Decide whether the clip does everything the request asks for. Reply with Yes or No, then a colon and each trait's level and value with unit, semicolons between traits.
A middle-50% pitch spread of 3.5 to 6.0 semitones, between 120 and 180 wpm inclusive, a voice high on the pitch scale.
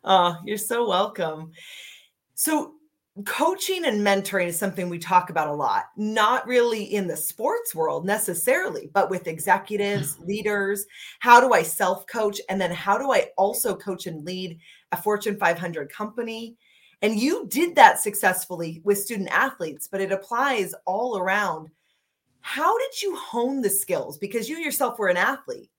Yes: average, 4.7 semitones; average, 160 wpm; high, 205 Hz